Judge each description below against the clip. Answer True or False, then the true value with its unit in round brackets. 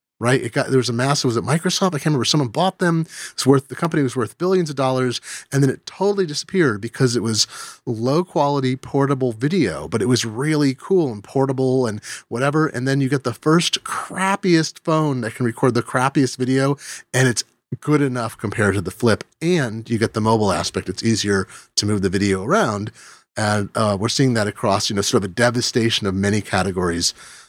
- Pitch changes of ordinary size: True (4.5 semitones)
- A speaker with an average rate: False (210 wpm)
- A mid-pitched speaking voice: False (130 Hz)